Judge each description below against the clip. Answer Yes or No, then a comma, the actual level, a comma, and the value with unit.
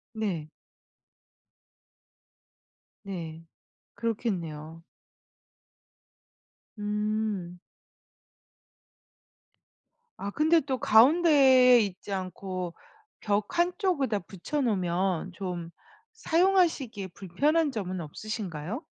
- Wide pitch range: Yes, wide, 6.8 semitones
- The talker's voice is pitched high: Yes, high, 205 Hz